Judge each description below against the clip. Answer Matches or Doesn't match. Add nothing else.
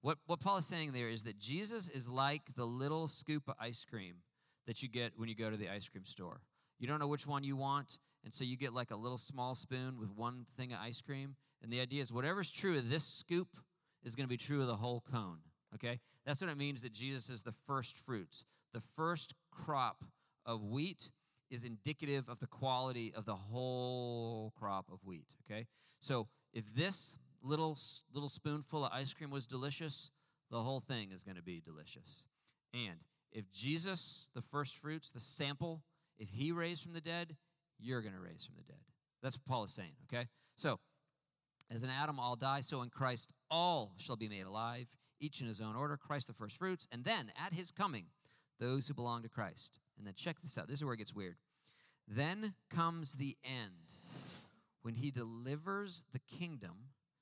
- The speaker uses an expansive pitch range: Doesn't match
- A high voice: Doesn't match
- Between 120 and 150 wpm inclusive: Doesn't match